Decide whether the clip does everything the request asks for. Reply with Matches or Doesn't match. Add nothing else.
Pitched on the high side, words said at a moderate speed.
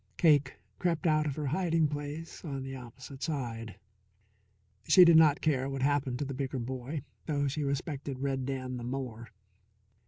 Doesn't match